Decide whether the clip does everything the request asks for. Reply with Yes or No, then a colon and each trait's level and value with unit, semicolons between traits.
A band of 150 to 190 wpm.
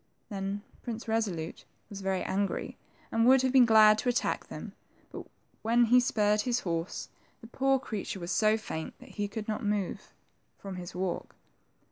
Yes: average, 170 wpm